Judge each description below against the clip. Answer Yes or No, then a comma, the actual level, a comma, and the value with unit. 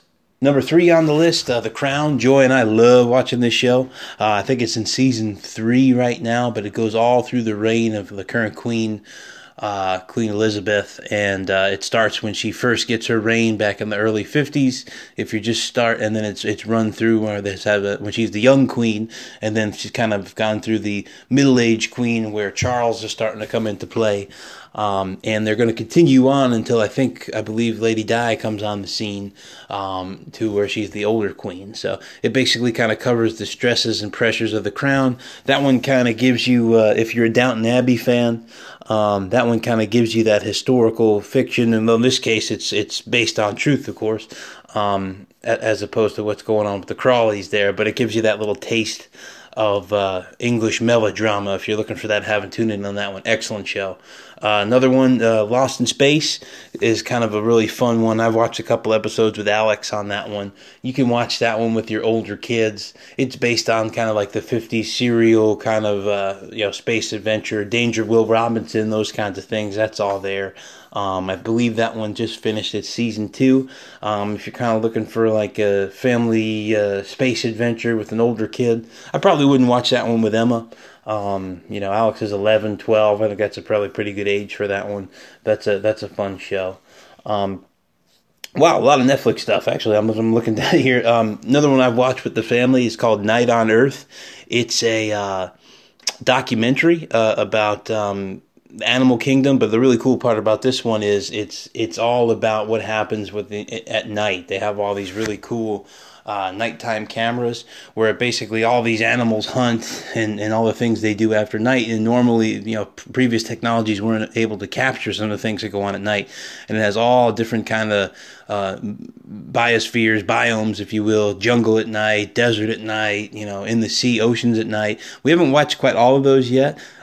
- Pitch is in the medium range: No, low, 110 Hz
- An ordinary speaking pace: No, fast, 210 wpm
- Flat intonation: Yes, narrow, 2.1 semitones